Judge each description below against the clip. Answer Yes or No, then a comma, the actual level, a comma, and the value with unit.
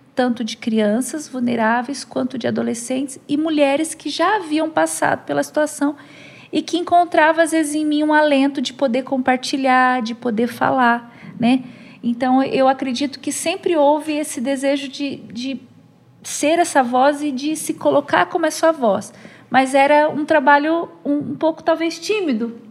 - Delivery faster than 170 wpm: No, average, 165 wpm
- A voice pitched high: Yes, very high, 280 Hz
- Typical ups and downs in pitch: Yes, average, 3.3 semitones